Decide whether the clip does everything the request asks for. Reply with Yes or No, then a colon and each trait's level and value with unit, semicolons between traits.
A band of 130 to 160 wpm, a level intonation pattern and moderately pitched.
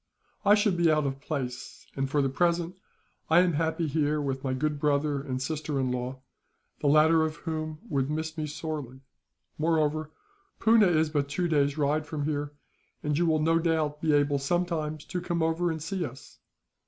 No: average, 190 wpm; narrow, 2.3 semitones; medium, 155 Hz